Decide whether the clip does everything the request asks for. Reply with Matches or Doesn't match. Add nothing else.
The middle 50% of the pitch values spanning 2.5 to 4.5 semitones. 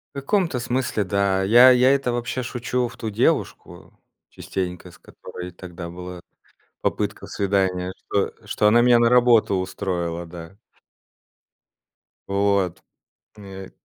Doesn't match